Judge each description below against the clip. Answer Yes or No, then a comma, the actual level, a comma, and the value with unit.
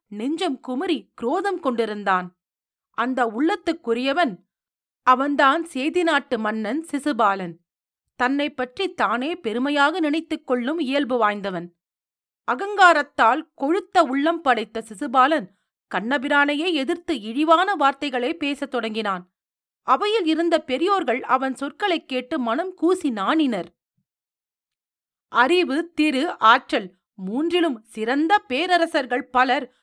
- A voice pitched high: Yes, very high, 280 Hz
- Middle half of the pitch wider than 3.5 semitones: Yes, average, 5.3 semitones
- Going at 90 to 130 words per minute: No, average, 80 wpm